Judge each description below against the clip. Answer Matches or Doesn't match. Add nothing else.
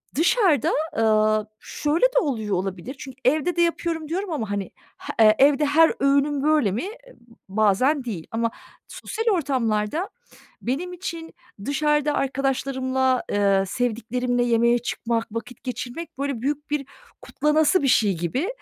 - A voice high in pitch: Matches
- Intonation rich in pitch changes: Doesn't match